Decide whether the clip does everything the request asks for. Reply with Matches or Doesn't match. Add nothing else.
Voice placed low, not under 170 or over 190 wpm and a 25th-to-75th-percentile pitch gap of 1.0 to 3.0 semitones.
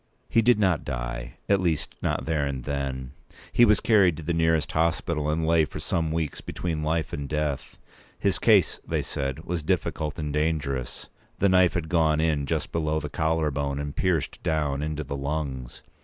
Matches